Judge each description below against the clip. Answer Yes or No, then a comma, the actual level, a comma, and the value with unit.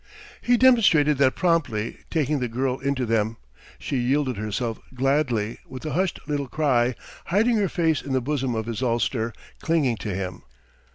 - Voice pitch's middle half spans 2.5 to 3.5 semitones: No, average, 4.7 semitones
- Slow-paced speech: No, average, 165 wpm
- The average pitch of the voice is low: Yes, low, 130 Hz